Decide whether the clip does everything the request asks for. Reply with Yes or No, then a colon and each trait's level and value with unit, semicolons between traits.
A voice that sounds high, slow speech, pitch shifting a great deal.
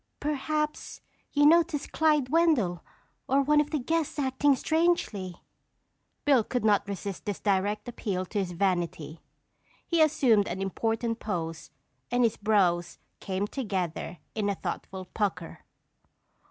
Yes: high, 220 Hz; slow, 130 wpm; wide, 7.4 semitones